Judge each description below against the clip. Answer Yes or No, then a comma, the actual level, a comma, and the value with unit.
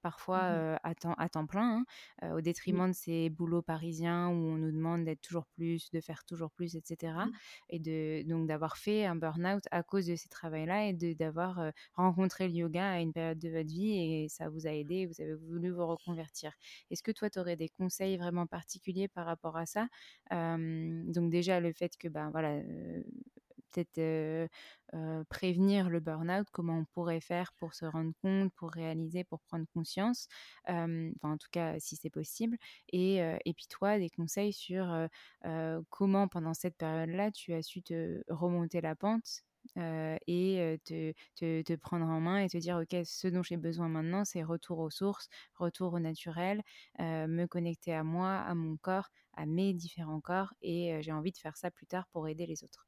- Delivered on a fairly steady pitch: Yes, narrow, 2.2 semitones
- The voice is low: No, medium, 170 Hz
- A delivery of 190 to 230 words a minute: Yes, average, 205 wpm